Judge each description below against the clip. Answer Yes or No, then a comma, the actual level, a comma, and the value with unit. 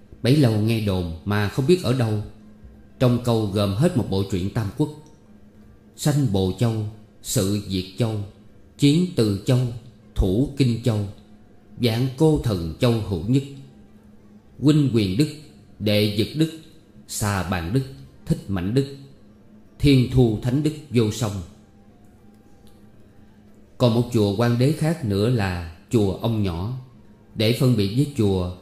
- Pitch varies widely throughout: No, average, 3.8 semitones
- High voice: No, low, 105 Hz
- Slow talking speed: Yes, slow, 145 wpm